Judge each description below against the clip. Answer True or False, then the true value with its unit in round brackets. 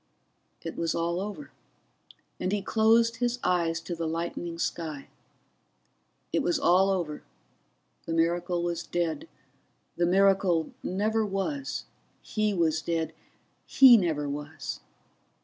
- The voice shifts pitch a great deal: False (4.0 semitones)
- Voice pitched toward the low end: False (175 Hz)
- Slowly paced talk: True (120 wpm)